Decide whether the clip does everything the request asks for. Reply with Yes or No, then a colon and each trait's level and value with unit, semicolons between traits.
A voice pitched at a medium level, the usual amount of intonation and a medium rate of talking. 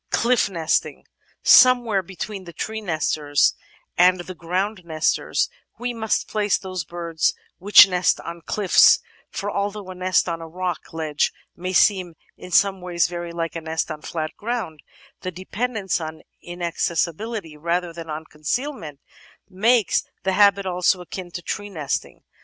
Yes: medium, 180 Hz; average, 3.4 semitones; average, 150 wpm